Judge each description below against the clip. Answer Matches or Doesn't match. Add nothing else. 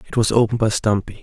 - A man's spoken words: Matches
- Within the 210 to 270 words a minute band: Matches